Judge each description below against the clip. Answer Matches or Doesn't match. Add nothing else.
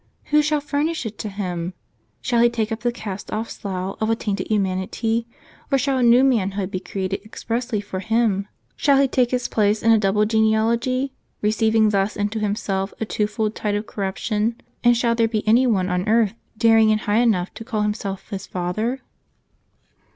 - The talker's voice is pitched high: Matches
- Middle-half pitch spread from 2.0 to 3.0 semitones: Matches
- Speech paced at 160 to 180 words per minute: Doesn't match